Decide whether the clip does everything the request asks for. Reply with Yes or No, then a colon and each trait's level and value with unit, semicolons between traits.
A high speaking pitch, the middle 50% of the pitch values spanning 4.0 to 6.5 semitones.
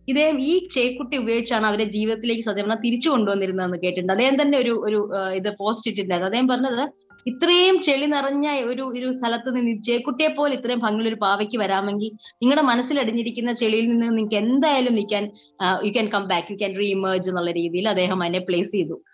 Yes: high, 225 Hz; average, 4.3 semitones